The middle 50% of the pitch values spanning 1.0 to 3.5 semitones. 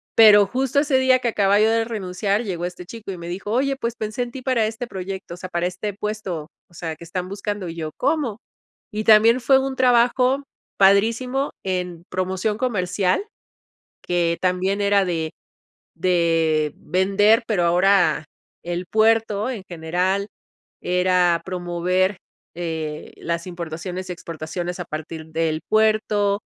No: average, 3.9 semitones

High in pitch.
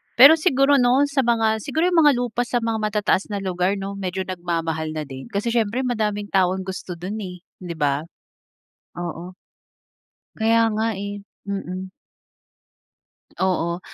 Yes: high, 205 Hz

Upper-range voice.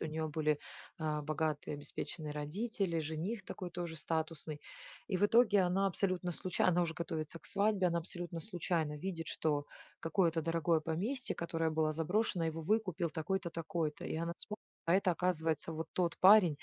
No: medium, 165 Hz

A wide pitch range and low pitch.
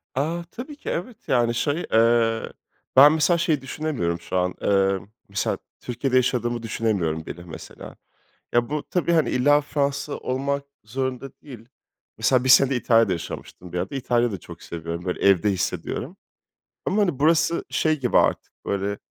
Yes: wide, 6.5 semitones; low, 125 Hz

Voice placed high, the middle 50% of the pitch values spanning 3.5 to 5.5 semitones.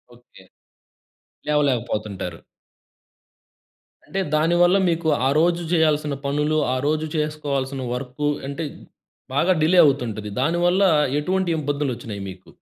No: medium, 150 Hz; average, 3.9 semitones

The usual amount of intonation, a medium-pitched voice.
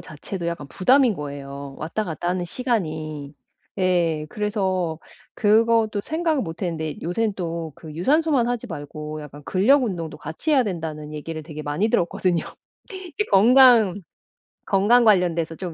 No: wide, 6.1 semitones; medium, 180 Hz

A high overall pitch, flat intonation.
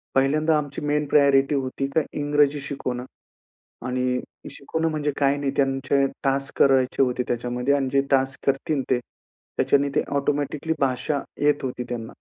No: medium, 140 Hz; narrow, 1.7 semitones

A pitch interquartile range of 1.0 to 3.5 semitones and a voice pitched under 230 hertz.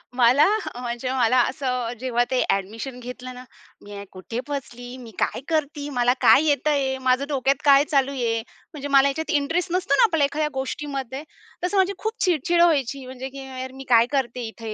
No: average, 2.8 semitones; very high, 265 Hz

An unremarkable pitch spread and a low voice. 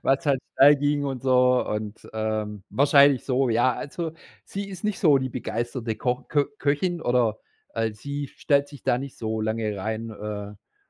Yes: average, 4.4 semitones; low, 125 Hz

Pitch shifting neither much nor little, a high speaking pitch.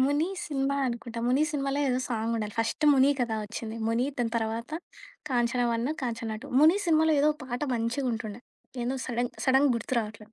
Yes: average, 3.3 semitones; high, 245 Hz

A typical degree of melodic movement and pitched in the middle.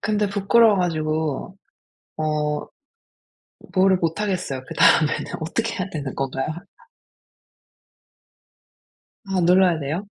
Yes: average, 4.2 semitones; medium, 175 Hz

